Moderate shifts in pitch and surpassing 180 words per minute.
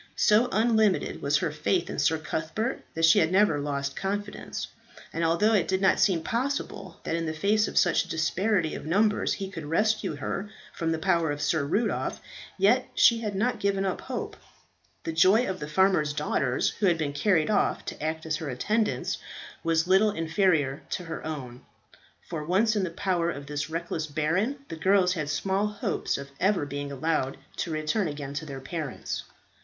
Yes: average, 4.7 semitones; average, 190 wpm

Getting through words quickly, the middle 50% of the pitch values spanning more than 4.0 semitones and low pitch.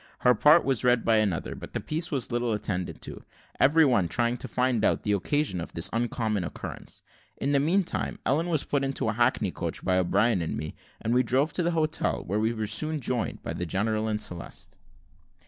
Yes: fast, 215 wpm; average, 5.0 semitones; low, 120 Hz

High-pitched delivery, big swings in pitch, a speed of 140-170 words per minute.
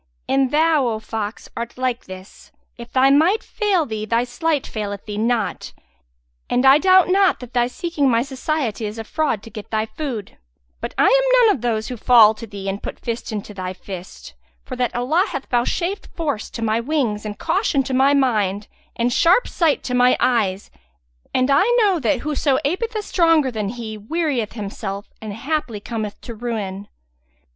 No: high, 245 Hz; wide, 5.8 semitones; average, 185 wpm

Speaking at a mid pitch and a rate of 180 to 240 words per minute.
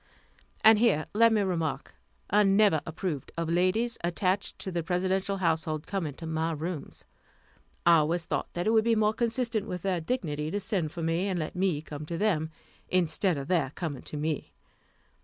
Yes: medium, 175 Hz; average, 185 wpm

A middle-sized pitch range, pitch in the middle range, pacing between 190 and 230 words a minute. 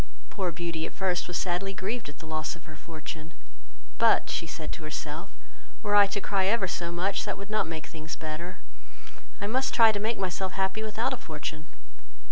Yes: average, 4.1 semitones; medium, 180 Hz; average, 200 wpm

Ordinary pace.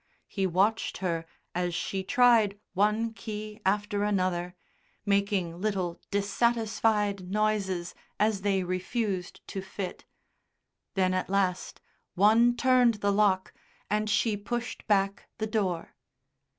No: slow, 115 wpm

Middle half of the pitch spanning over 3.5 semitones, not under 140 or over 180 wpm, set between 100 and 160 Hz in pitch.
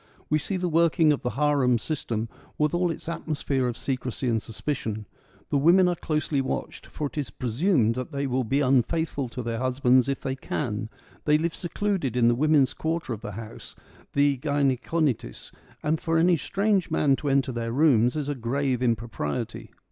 No: average, 4.2 semitones; average, 195 wpm; medium, 140 Hz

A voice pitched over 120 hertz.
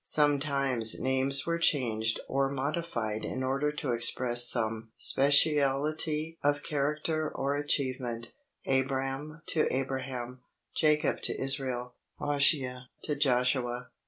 Yes: low, 135 Hz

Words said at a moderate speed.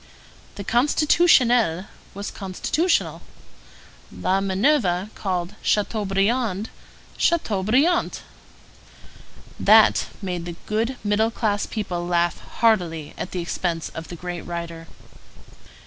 No: slow, 100 wpm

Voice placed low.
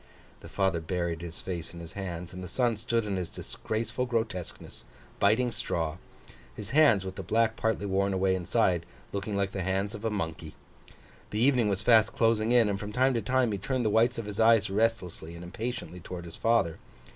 Yes: low, 100 Hz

